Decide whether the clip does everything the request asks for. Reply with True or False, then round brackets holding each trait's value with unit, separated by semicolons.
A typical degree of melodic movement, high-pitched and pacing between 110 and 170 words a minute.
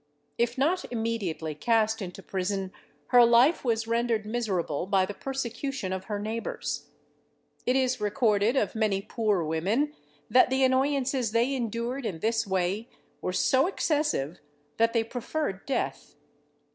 True (4.4 semitones; 230 Hz; 140 wpm)